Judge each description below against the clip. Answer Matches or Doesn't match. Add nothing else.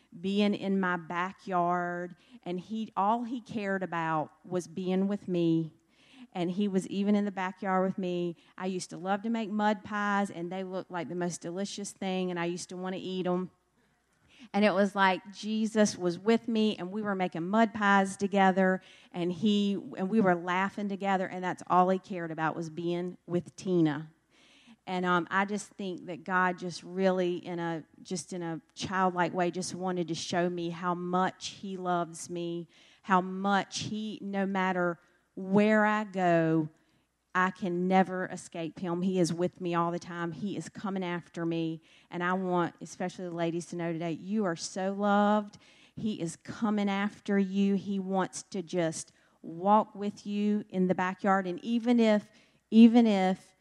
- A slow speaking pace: Doesn't match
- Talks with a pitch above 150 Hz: Matches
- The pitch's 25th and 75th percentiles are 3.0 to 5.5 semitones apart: Doesn't match